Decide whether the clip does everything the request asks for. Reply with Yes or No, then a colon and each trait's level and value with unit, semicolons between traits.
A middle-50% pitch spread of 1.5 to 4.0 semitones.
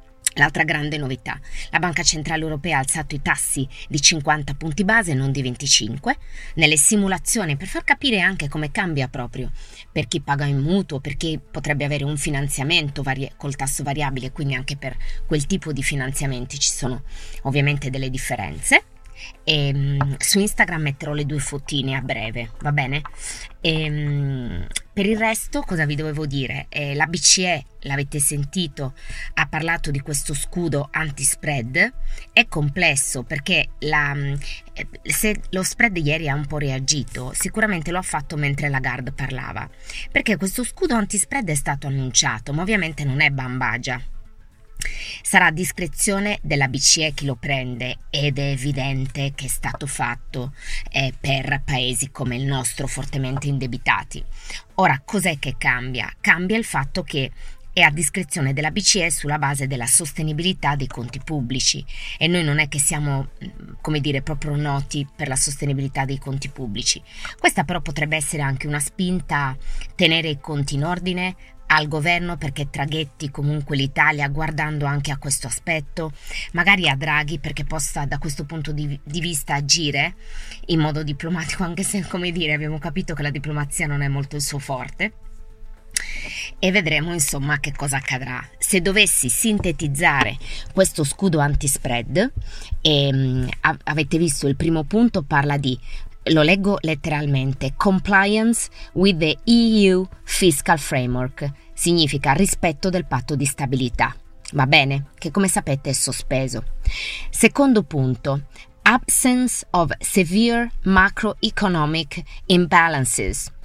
Yes: average, 3.7 semitones